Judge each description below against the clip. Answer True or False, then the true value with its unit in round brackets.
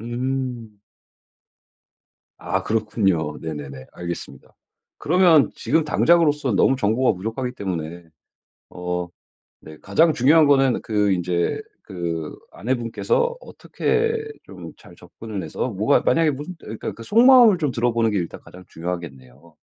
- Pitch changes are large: True (8.3 semitones)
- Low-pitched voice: True (115 Hz)